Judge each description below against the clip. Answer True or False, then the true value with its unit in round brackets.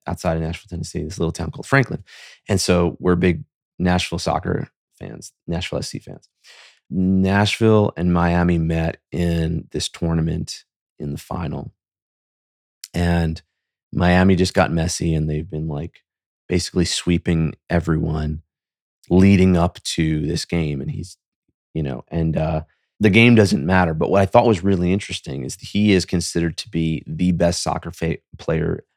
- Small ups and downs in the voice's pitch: True (2.1 semitones)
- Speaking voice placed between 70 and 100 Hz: True (85 Hz)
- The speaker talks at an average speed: True (155 wpm)